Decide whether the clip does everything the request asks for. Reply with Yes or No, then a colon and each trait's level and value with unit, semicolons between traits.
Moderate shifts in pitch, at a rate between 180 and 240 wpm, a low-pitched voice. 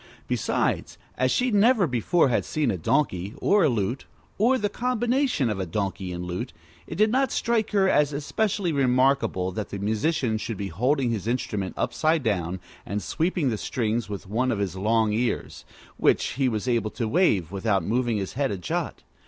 No: wide, 8.0 semitones; average, 185 wpm; low, 120 Hz